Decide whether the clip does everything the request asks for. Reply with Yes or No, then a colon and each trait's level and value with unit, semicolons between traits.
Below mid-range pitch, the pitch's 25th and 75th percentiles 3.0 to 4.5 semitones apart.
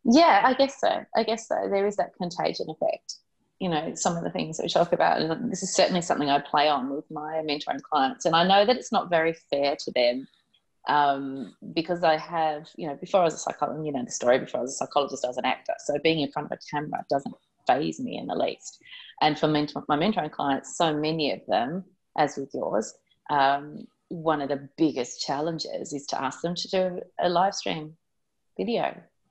No: medium, 155 Hz; average, 4.1 semitones